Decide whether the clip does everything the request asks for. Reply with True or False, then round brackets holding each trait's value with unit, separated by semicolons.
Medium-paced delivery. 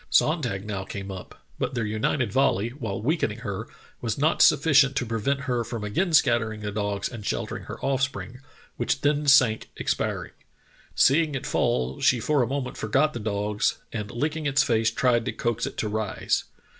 True (180 wpm)